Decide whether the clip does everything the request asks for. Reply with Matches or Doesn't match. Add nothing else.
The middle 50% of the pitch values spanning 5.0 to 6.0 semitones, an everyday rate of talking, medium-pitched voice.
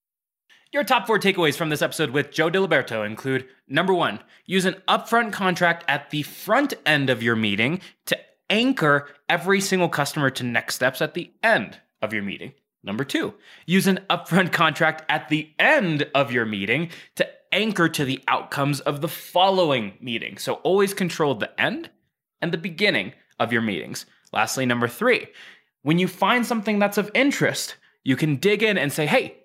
Matches